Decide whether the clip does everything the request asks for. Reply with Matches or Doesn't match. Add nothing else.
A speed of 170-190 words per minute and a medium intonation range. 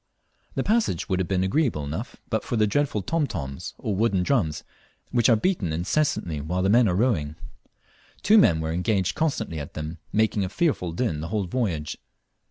Doesn't match